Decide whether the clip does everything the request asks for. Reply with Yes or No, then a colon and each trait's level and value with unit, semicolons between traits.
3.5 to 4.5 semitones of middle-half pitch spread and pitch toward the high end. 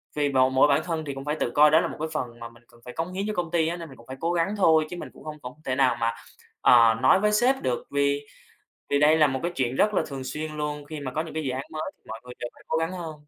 No: average, 3.9 semitones; medium, 150 Hz